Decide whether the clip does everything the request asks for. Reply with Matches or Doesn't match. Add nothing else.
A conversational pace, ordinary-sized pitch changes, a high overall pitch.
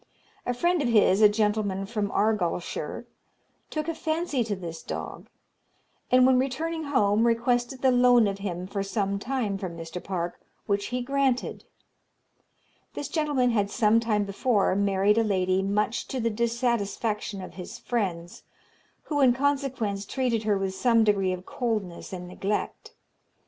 Matches